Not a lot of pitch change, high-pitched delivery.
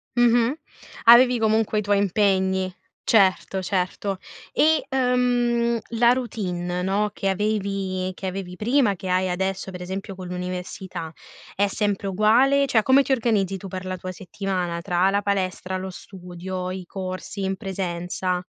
No: average, 3.0 semitones; high, 195 Hz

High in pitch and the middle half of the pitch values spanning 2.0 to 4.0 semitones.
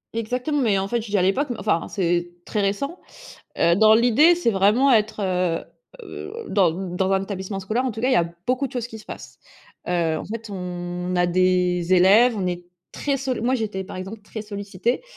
No: high, 200 Hz; average, 4.4 semitones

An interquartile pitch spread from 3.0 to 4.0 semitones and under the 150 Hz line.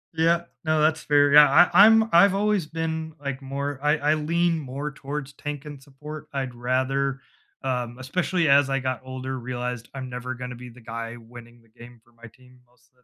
Yes: average, 3.6 semitones; low, 135 Hz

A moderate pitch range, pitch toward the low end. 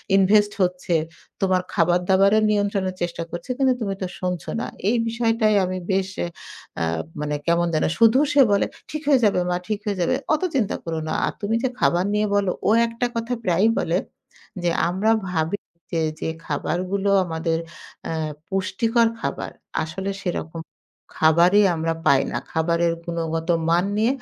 No: average, 3.9 semitones; high, 190 Hz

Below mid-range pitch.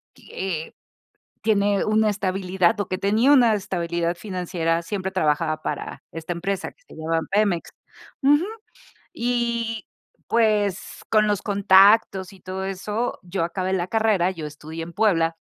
No: high, 190 Hz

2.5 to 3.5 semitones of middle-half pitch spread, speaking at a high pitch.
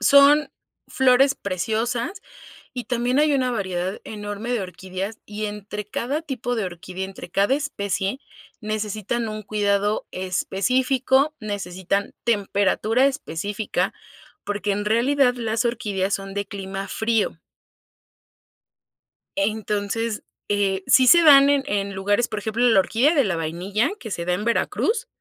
No: average, 4.0 semitones; high, 215 Hz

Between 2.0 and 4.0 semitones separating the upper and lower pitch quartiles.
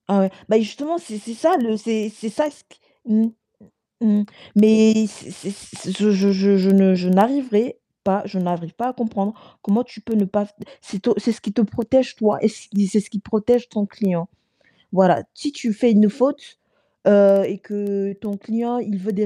Yes: narrow, 2.5 semitones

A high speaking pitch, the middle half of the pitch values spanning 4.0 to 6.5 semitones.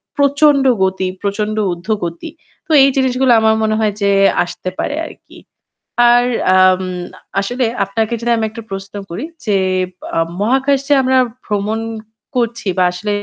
Yes: high, 220 Hz; average, 4.7 semitones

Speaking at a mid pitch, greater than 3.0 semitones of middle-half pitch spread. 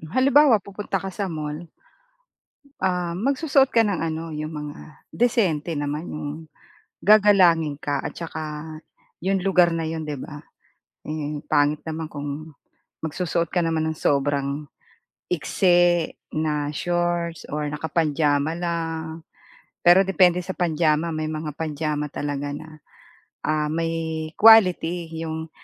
No: medium, 160 Hz; average, 2.7 semitones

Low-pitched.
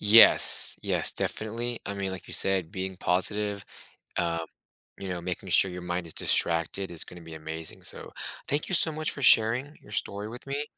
Yes: very low, 95 Hz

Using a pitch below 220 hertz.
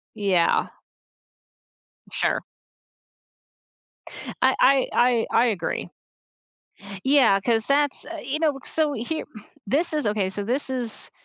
No: very high, 250 Hz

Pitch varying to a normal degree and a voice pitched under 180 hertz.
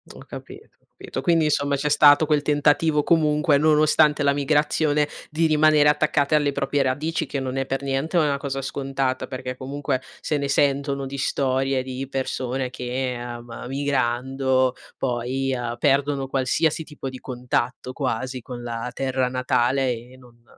No: narrow, 2.3 semitones; low, 135 Hz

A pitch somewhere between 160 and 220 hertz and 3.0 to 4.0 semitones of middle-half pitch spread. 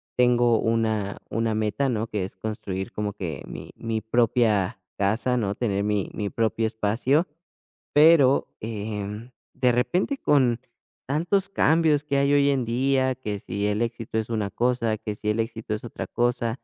No: low, 115 Hz; average, 3.3 semitones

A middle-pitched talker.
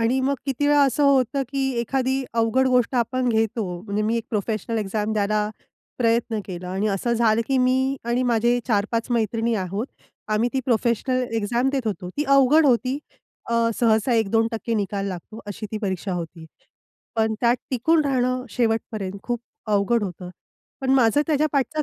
No: high, 230 Hz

